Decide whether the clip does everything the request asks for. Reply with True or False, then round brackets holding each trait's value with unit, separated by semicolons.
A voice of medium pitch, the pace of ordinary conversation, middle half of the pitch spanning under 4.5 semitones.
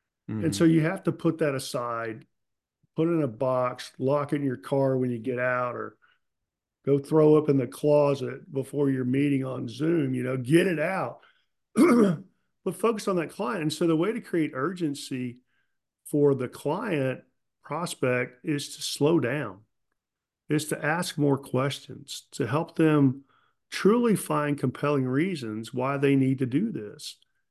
True (145 Hz; 170 wpm; 3.3 semitones)